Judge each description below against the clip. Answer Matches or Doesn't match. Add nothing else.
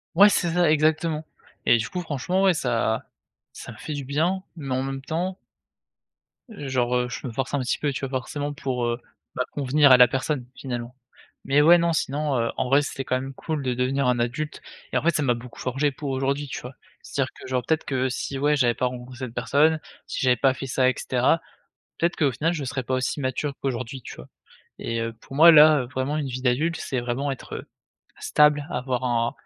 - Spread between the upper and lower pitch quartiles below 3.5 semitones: Matches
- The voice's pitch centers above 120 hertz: Matches